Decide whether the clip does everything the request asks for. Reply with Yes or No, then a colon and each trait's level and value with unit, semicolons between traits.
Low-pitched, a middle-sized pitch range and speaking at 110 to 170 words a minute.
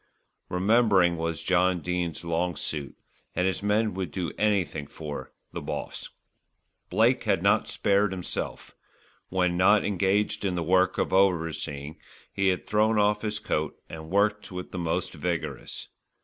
Yes: very low, 90 Hz; average, 3.4 semitones; average, 150 wpm